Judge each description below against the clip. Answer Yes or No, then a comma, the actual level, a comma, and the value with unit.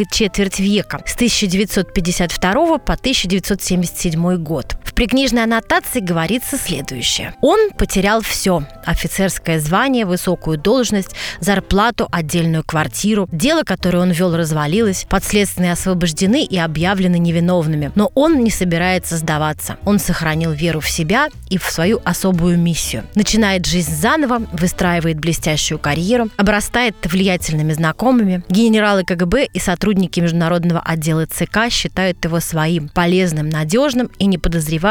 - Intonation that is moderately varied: Yes, average, 3.7 semitones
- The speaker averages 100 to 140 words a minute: Yes, average, 120 wpm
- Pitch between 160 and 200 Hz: Yes, medium, 185 Hz